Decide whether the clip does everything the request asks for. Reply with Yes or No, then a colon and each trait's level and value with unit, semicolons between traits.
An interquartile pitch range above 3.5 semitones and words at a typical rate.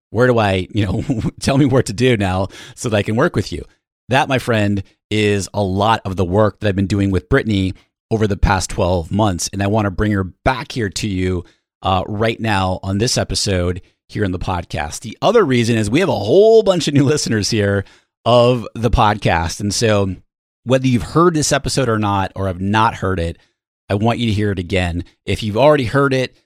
No: average, 4.0 semitones; fast, 225 wpm